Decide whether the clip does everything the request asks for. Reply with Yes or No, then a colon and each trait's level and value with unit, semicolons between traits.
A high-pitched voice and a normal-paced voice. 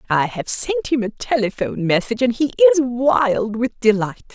Yes: high, 220 Hz; average, 180 wpm